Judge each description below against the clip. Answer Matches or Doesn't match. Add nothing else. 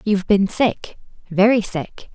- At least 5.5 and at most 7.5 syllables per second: Doesn't match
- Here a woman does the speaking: Matches